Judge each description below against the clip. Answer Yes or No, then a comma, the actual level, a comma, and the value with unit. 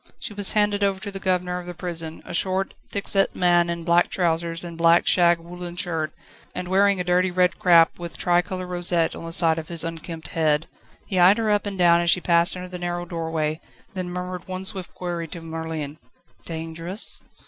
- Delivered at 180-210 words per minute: Yes, fast, 205 wpm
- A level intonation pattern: Yes, narrow, 1.8 semitones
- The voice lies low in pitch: No, medium, 175 Hz